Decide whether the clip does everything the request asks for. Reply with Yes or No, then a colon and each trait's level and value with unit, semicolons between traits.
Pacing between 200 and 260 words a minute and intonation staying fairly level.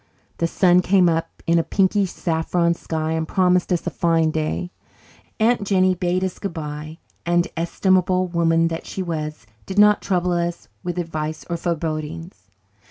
No: average, 160 wpm; narrow, 2.0 semitones